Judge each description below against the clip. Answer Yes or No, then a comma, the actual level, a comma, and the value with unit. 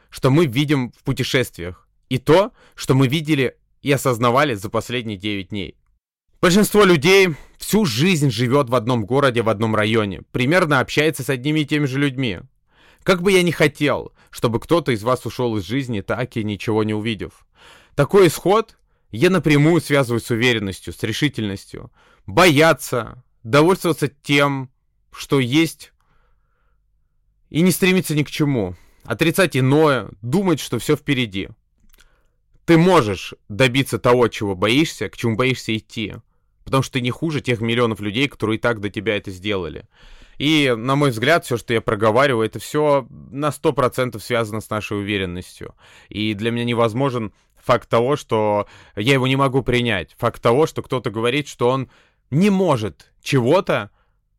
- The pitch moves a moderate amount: Yes, average, 4.8 semitones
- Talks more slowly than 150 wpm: No, average, 155 wpm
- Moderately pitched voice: No, low, 125 Hz